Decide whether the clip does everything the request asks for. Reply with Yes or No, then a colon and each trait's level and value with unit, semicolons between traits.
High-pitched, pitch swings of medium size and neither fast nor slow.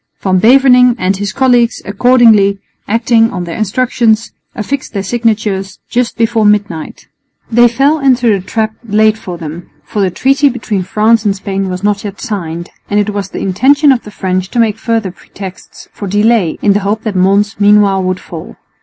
Yes: high, 210 Hz; average, 3.3 semitones; average, 180 wpm